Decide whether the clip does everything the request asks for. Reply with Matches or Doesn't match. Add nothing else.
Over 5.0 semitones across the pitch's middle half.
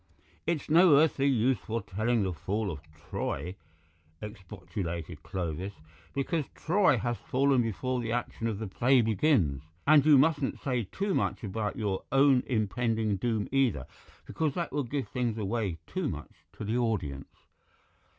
Matches